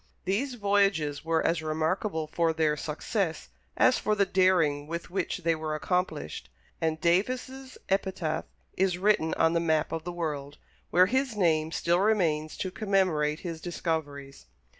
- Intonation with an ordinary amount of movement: Yes, average, 3.6 semitones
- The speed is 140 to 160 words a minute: Yes, average, 150 wpm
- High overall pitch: No, medium, 170 Hz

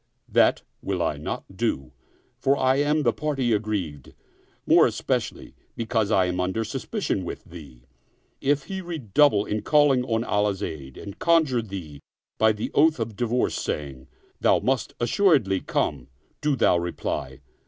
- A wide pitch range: Yes, wide, 7.1 semitones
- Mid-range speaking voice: No, low, 110 Hz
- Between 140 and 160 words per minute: Yes, average, 150 wpm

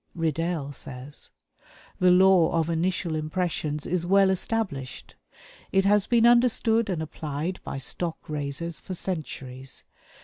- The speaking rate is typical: No, slow, 125 wpm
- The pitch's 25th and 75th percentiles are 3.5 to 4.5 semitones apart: Yes, average, 4.1 semitones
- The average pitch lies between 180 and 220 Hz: No, medium, 170 Hz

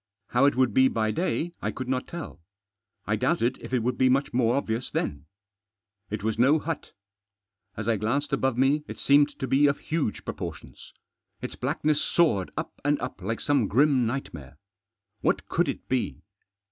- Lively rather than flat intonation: No, average, 4.1 semitones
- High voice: No, low, 130 Hz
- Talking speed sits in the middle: Yes, average, 180 wpm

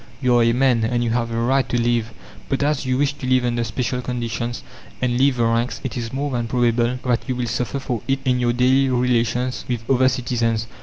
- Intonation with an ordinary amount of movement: No, narrow, 1.6 semitones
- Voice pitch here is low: Yes, low, 125 Hz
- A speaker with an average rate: No, fast, 235 wpm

